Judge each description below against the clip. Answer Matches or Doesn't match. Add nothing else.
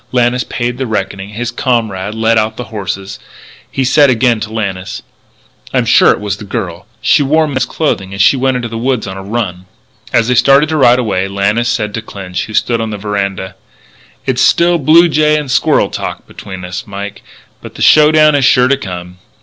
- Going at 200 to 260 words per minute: Matches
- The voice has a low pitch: Matches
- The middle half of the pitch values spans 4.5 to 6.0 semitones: Matches